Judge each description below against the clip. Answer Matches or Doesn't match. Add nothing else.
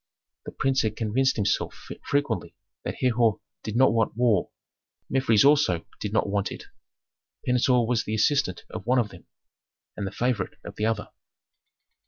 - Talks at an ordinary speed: Matches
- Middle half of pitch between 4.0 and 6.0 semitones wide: Doesn't match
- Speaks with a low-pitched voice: Matches